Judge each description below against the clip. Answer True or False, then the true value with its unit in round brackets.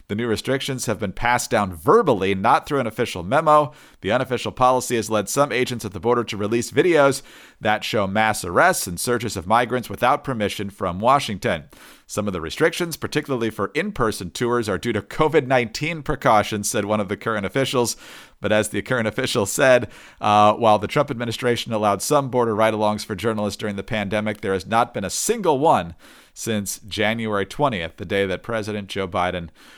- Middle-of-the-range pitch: False (110 Hz)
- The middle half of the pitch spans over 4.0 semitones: False (3.5 semitones)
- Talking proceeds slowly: False (185 wpm)